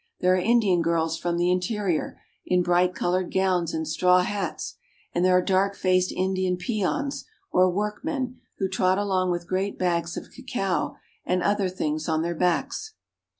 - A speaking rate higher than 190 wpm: No, average, 165 wpm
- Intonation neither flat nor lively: No, narrow, 2.0 semitones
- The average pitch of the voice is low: No, medium, 185 Hz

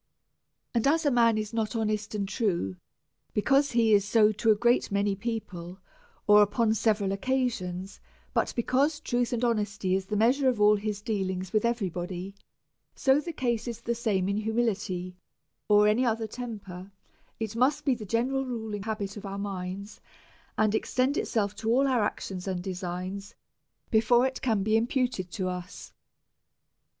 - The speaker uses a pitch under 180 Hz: No, high, 215 Hz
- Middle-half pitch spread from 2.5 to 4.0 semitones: Yes, average, 3.2 semitones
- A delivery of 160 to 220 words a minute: Yes, average, 175 wpm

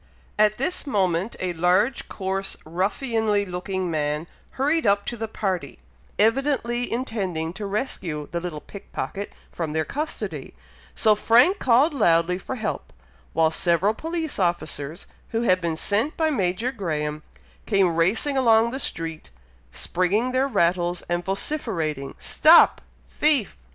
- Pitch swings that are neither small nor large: No, wide, 5.8 semitones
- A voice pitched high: Yes, high, 200 Hz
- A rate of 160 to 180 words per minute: No, slow, 135 wpm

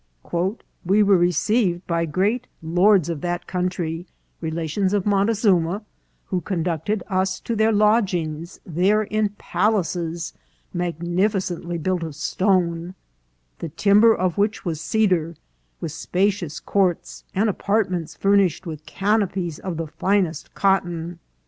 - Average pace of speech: No, slow, 125 wpm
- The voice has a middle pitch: Yes, medium, 180 Hz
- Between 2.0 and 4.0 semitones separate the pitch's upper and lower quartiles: Yes, average, 3.2 semitones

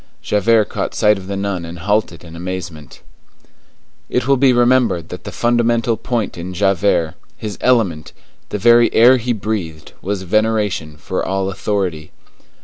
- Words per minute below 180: Yes, average, 150 wpm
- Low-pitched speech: Yes, low, 100 Hz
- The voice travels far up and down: No, average, 4.6 semitones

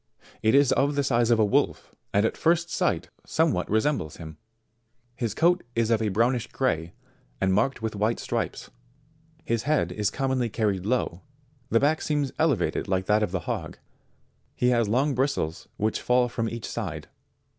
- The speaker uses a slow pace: No, average, 175 wpm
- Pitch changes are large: No, average, 4.3 semitones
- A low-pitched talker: Yes, low, 115 Hz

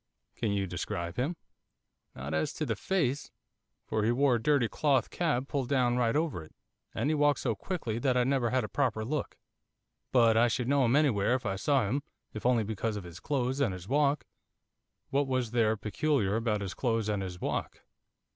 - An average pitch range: Yes, average, 4.6 semitones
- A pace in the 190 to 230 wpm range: Yes, fast, 205 wpm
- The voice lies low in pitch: Yes, low, 120 Hz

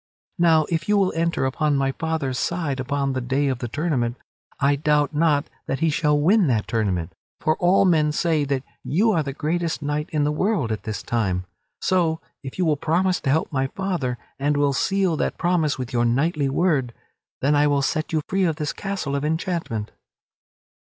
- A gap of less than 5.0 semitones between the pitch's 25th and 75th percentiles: Yes, average, 3.7 semitones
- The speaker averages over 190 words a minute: Yes, average, 200 wpm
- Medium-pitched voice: Yes, medium, 150 Hz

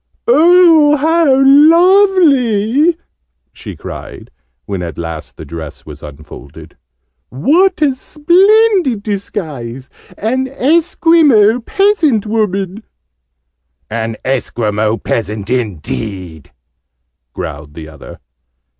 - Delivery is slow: Yes, slow, 85 wpm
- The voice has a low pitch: No, high, 220 Hz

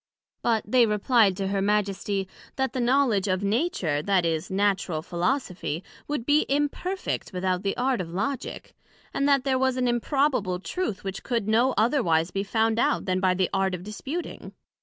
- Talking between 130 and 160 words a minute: No, average, 175 wpm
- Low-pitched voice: No, high, 210 Hz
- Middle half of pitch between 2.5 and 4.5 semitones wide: No, wide, 5.6 semitones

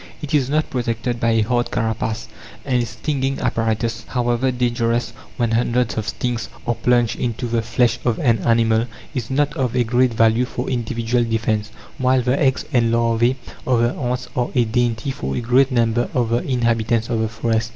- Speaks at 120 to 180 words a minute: No, average, 190 wpm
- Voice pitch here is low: Yes, low, 120 Hz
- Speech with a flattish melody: Yes, narrow, 1.6 semitones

